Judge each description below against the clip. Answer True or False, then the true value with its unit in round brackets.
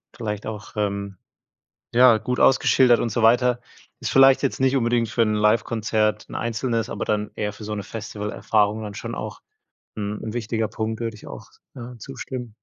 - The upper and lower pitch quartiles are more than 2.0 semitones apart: True (2.4 semitones)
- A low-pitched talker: True (110 Hz)